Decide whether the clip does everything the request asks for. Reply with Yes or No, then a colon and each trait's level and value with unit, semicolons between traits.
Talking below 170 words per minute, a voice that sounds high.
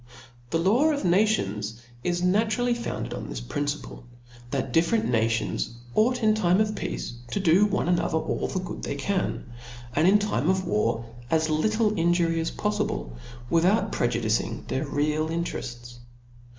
No: average, 150 wpm; medium, 170 Hz